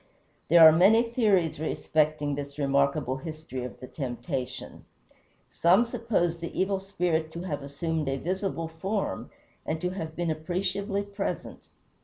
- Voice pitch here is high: No, medium, 165 Hz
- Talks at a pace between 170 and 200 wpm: No, average, 140 wpm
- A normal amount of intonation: Yes, average, 4.6 semitones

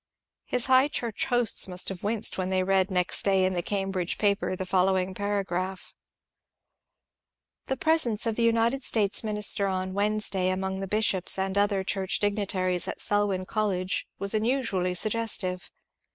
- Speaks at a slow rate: No, average, 155 wpm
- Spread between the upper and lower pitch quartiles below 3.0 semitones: Yes, narrow, 2.5 semitones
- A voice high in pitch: Yes, high, 195 Hz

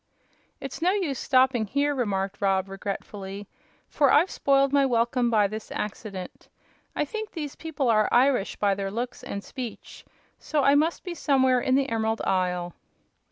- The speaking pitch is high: Yes, high, 245 Hz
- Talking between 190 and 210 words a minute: No, average, 160 wpm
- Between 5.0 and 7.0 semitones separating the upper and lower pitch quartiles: Yes, wide, 5.6 semitones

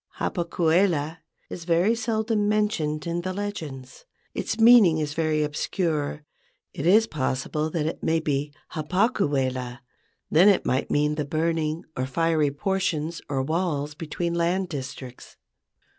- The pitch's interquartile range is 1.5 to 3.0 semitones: No, average, 3.8 semitones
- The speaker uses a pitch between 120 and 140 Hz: No, medium, 160 Hz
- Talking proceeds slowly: No, average, 145 wpm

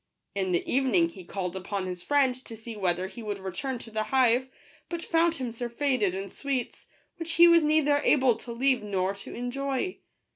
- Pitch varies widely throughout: Yes, wide, 5.9 semitones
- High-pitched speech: Yes, high, 240 Hz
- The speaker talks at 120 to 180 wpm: No, average, 190 wpm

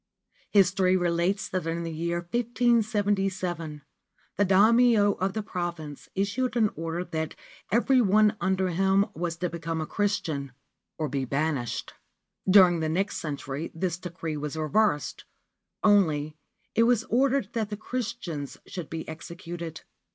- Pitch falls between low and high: Yes, medium, 180 Hz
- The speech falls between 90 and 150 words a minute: Yes, slow, 135 wpm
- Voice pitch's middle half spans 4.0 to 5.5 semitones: Yes, average, 4.3 semitones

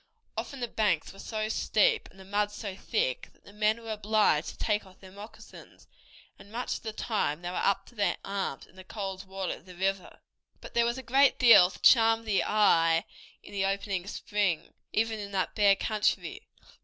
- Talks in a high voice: Yes, high, 205 Hz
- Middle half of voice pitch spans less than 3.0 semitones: Yes, narrow, 2.6 semitones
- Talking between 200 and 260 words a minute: Yes, fast, 205 wpm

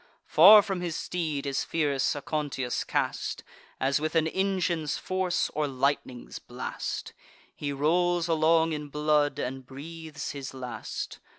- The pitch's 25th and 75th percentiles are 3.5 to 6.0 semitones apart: No, average, 3.1 semitones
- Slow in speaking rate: Yes, slow, 130 wpm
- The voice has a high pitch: No, medium, 155 Hz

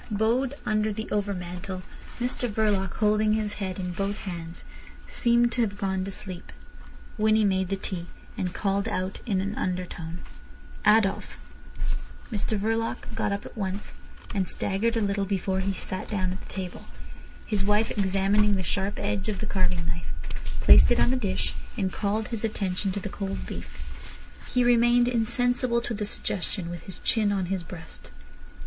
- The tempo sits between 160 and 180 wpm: Yes, average, 170 wpm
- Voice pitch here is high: Yes, high, 200 Hz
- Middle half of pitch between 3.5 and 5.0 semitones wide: No, narrow, 2.5 semitones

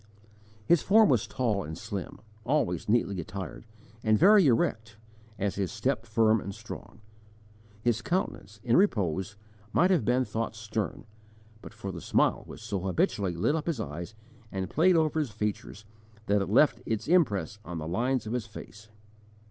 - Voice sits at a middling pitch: No, low, 110 Hz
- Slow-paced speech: No, average, 165 wpm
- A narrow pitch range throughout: No, average, 4.6 semitones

